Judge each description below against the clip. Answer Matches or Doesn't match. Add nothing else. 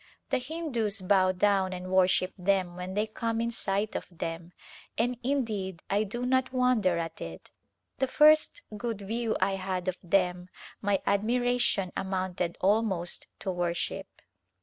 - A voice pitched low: Doesn't match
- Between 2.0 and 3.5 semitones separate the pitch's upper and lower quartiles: Doesn't match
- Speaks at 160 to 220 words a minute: Doesn't match